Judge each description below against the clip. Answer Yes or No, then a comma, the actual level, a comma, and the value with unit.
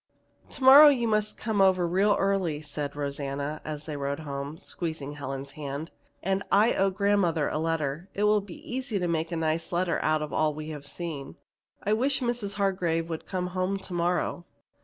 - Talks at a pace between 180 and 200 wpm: Yes, average, 185 wpm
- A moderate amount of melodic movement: Yes, average, 4.7 semitones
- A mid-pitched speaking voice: Yes, medium, 170 Hz